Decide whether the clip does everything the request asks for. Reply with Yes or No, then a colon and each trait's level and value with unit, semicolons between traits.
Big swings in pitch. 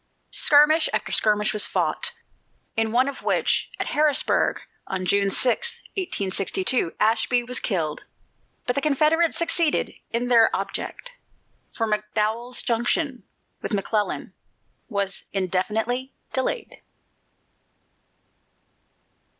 No: average, 5.0 semitones